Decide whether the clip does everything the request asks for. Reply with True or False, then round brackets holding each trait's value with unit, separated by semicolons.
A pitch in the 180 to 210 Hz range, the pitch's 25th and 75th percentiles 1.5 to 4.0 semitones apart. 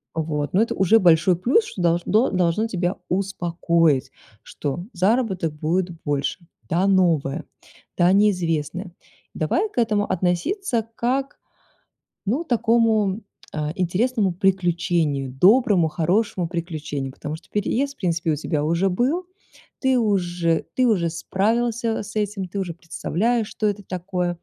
False (185 Hz; 4.6 semitones)